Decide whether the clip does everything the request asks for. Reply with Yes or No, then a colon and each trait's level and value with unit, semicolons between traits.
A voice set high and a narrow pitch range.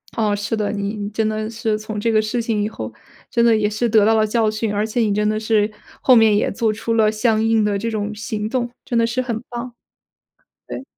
Yes: high, 215 Hz; narrow, 1.4 semitones